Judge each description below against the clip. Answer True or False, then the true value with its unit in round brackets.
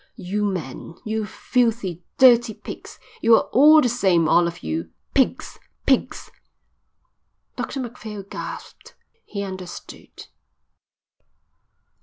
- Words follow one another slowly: True (100 wpm)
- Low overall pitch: False (210 Hz)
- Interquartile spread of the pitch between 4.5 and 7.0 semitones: True (5.2 semitones)